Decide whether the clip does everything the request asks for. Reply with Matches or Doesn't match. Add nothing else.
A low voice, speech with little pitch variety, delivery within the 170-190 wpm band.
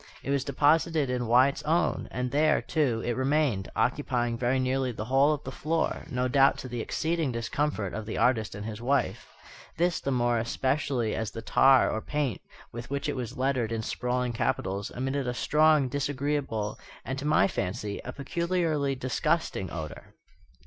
Doesn't match